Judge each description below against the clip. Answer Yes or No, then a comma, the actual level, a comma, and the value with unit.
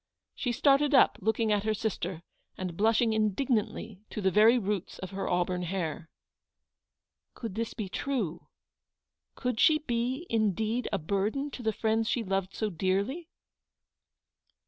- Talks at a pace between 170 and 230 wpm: No, average, 145 wpm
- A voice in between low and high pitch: No, high, 215 Hz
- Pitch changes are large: No, average, 3.8 semitones